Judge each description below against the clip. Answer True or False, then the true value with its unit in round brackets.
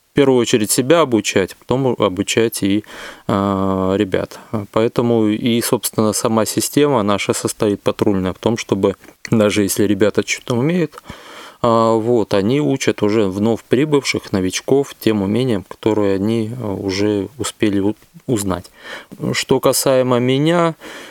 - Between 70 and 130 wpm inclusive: True (120 wpm)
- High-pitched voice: False (110 Hz)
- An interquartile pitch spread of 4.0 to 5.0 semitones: False (3.5 semitones)